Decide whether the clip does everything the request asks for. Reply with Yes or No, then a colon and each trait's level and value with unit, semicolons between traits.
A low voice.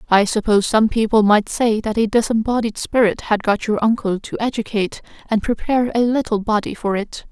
No: high, 220 Hz